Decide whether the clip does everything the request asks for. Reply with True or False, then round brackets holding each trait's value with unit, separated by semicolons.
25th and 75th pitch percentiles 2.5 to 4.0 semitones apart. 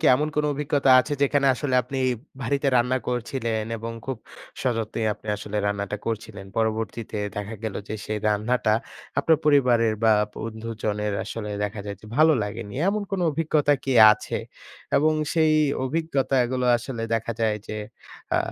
False (4.4 semitones)